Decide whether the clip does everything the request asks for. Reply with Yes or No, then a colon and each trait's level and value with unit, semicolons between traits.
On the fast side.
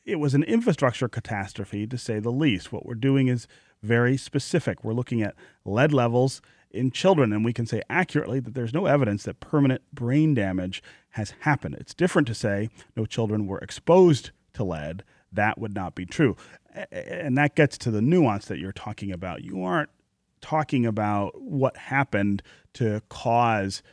No: average, 175 wpm